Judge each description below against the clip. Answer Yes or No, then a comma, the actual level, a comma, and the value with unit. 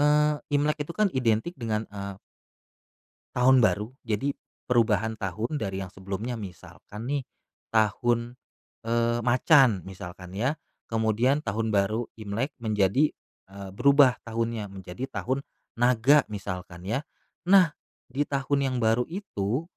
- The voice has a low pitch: Yes, low, 115 Hz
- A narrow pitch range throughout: No, average, 4.8 semitones